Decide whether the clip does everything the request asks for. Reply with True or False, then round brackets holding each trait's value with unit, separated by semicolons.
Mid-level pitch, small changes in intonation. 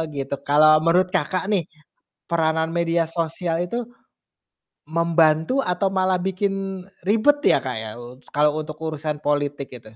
False (165 Hz; 3.2 semitones)